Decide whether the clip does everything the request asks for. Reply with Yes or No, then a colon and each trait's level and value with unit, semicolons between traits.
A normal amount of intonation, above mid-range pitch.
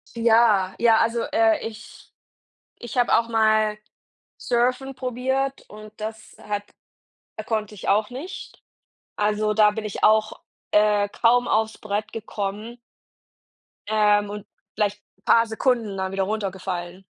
No: narrow, 2.1 semitones; high, 215 Hz